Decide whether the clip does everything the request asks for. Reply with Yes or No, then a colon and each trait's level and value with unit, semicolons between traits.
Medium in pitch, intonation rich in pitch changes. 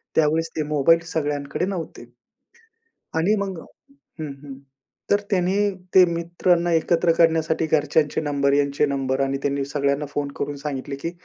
No: medium, 150 Hz; average, 2.9 semitones